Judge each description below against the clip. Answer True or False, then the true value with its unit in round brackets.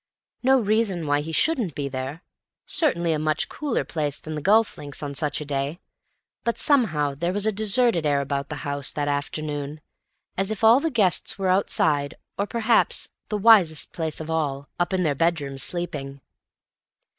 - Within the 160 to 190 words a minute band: True (170 wpm)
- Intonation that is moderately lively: False (6.2 semitones)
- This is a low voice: False (160 Hz)